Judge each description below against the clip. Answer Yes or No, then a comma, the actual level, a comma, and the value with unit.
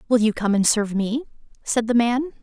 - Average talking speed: No, fast, 225 wpm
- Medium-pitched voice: No, high, 230 Hz